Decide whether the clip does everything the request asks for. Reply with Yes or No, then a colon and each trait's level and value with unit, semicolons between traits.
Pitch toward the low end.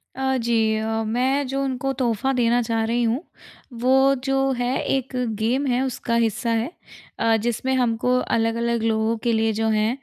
No: high, 235 Hz